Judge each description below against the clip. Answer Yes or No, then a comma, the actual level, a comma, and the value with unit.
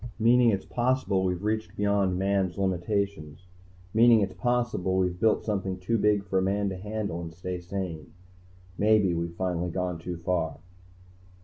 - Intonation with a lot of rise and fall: No, average, 2.9 semitones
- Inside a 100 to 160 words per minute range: Yes, average, 155 wpm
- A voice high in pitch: No, very low, 95 Hz